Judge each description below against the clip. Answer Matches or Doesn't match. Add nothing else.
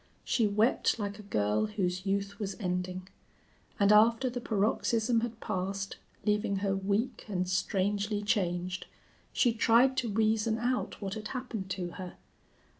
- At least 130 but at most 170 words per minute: Matches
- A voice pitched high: Matches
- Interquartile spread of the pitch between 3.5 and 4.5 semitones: Doesn't match